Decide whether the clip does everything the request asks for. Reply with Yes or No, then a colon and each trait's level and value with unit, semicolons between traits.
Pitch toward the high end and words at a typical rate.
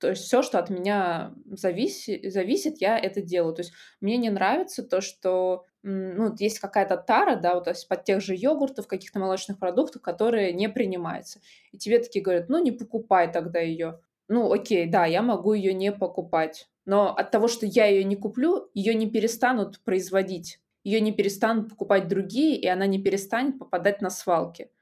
No: high, 200 Hz; fast, 185 wpm